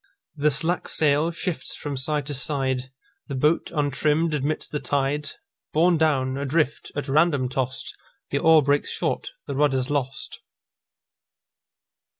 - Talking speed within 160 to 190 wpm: No, slow, 135 wpm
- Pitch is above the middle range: No, medium, 145 Hz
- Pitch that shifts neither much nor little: No, narrow, 2.3 semitones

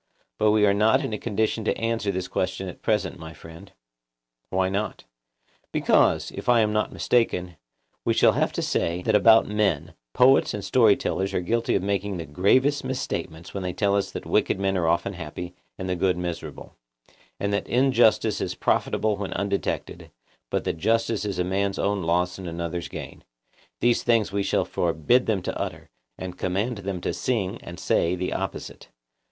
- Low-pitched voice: Yes, low, 100 Hz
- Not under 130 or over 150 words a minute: No, average, 185 wpm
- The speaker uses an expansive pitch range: No, average, 3.4 semitones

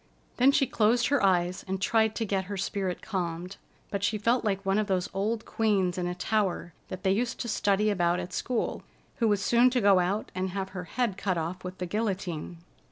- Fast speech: Yes, fast, 220 wpm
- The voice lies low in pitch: No, high, 195 Hz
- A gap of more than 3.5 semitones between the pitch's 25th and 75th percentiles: No, average, 3.2 semitones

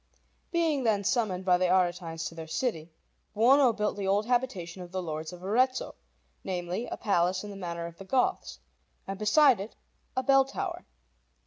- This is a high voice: Yes, high, 195 Hz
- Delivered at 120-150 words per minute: No, average, 180 wpm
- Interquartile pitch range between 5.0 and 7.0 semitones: Yes, wide, 5.6 semitones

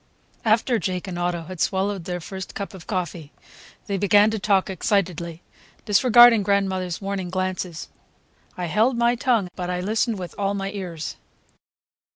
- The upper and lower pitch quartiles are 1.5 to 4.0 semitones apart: Yes, narrow, 2.6 semitones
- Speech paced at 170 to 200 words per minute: No, average, 155 wpm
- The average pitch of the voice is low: No, high, 190 Hz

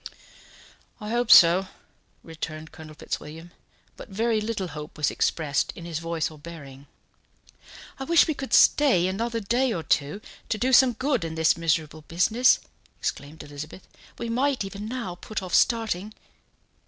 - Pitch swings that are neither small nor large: No, wide, 6.5 semitones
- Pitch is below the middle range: No, medium, 185 Hz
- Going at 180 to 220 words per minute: No, average, 155 wpm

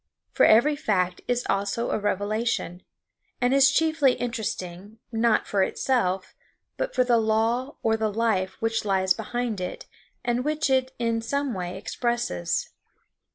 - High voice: Yes, high, 225 Hz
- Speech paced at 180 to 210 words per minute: No, average, 145 wpm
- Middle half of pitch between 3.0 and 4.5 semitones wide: Yes, average, 3.8 semitones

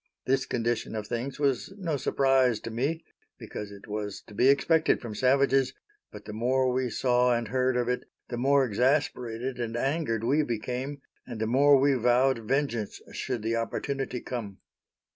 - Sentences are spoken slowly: No, average, 170 wpm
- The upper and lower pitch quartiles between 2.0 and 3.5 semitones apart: Yes, average, 2.8 semitones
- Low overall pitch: Yes, low, 125 Hz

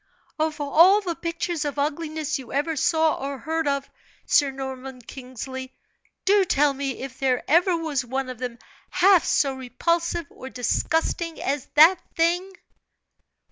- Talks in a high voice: Yes, very high, 290 Hz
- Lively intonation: No, average, 3.9 semitones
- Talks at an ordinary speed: Yes, average, 145 wpm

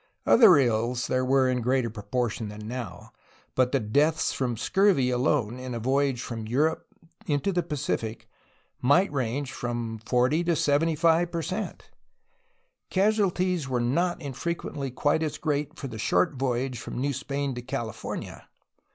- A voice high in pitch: No, low, 130 Hz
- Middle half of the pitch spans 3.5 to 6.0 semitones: Yes, average, 4.3 semitones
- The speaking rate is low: No, average, 150 wpm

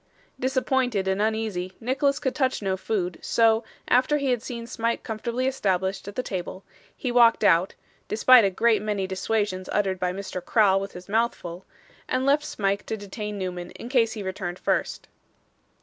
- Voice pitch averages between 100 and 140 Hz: No, high, 215 Hz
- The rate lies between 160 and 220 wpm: Yes, average, 175 wpm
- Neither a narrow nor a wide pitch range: Yes, average, 4.3 semitones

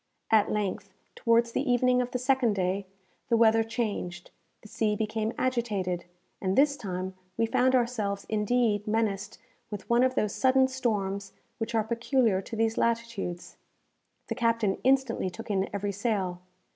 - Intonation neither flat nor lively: Yes, average, 3.2 semitones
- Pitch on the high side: Yes, high, 220 Hz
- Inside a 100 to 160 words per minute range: Yes, average, 155 wpm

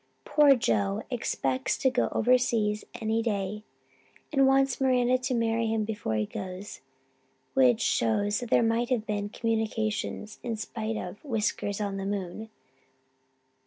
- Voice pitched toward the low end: No, high, 220 Hz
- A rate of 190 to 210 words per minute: No, slow, 135 wpm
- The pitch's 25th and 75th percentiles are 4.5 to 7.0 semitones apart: No, average, 2.9 semitones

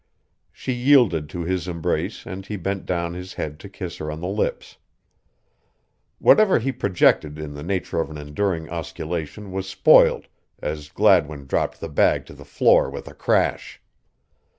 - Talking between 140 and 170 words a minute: Yes, average, 165 wpm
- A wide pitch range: No, average, 4.0 semitones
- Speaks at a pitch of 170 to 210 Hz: No, very low, 85 Hz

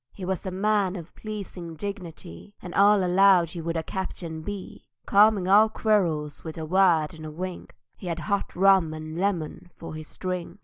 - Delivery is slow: No, average, 180 wpm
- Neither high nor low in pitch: Yes, medium, 180 Hz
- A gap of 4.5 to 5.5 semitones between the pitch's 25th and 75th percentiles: No, average, 3.4 semitones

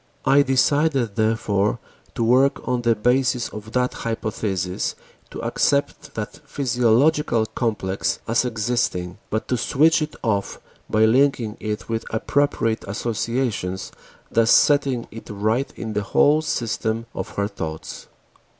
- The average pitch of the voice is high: No, low, 115 Hz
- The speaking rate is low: Yes, slow, 130 wpm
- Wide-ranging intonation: No, average, 3.6 semitones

